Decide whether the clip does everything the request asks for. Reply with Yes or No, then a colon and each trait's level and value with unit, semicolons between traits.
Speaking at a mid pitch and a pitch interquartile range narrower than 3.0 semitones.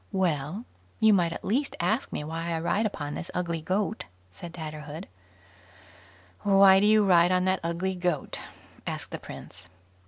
No: medium, 180 Hz; average, 3.3 semitones